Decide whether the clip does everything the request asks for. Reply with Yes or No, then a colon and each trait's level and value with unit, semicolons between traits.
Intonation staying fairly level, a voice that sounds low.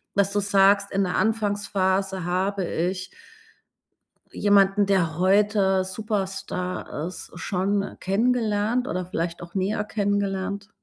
No: narrow, 1.6 semitones; high, 195 Hz